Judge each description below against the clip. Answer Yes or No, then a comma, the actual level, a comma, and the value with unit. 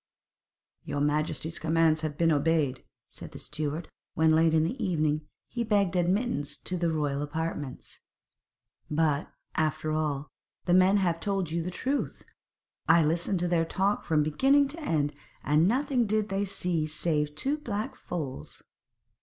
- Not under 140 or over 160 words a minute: Yes, average, 155 wpm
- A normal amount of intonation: Yes, average, 4.2 semitones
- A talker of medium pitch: Yes, medium, 165 Hz